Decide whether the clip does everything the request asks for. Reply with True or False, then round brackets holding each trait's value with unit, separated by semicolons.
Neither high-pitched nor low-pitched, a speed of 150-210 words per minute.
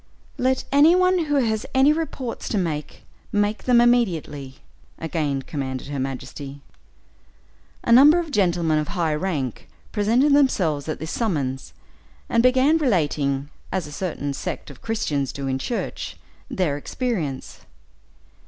False (180 Hz; 135 wpm)